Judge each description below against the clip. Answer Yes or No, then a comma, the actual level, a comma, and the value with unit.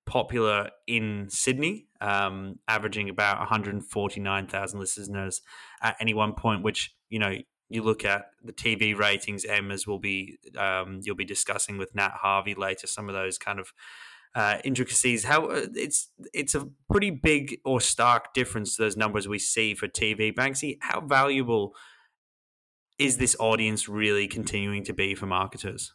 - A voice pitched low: Yes, low, 105 Hz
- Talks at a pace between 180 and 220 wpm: No, average, 165 wpm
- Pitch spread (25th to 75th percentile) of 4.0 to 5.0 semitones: No, average, 2.8 semitones